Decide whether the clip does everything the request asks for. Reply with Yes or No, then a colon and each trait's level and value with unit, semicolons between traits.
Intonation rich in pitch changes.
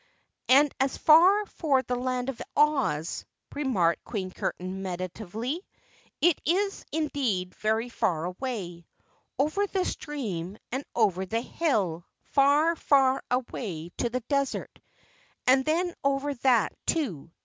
Yes: wide, 7.4 semitones